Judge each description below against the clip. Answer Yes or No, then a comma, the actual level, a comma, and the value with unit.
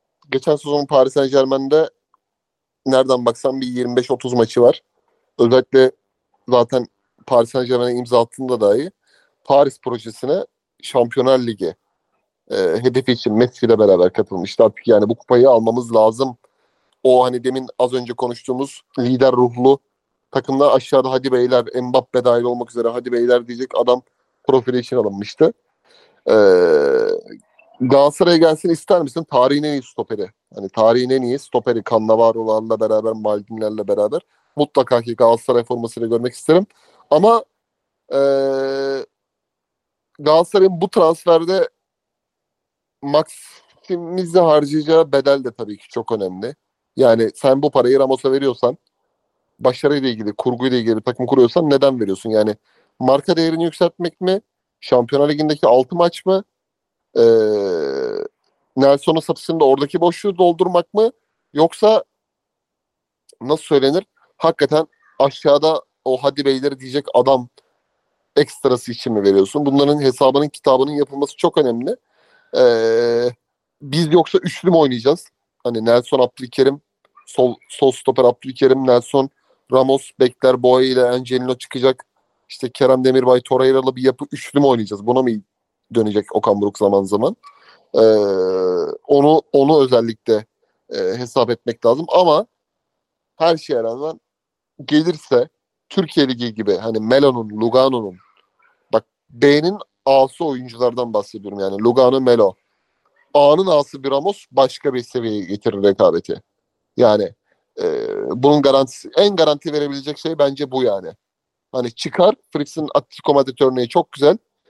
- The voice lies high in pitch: No, low, 135 Hz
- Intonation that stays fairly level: No, average, 4.4 semitones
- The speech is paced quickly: No, average, 125 wpm